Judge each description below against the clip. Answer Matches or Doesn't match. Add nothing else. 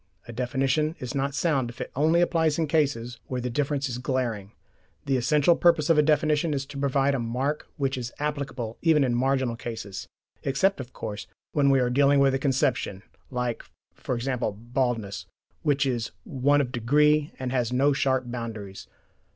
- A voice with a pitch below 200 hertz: Matches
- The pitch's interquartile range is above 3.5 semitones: Doesn't match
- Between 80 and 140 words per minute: Doesn't match